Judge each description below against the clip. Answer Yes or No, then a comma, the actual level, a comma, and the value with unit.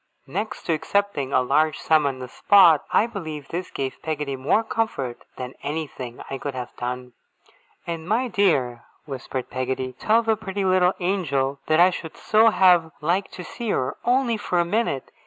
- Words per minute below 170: No, average, 175 wpm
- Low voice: No, medium, 160 Hz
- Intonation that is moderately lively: No, wide, 6.9 semitones